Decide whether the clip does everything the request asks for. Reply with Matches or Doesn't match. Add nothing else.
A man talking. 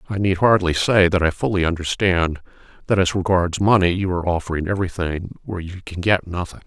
Matches